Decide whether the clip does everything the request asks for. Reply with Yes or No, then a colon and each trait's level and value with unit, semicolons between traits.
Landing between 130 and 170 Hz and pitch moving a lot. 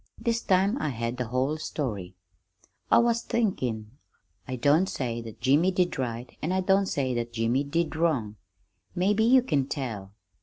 Yes: medium, 140 Hz; wide, 7.8 semitones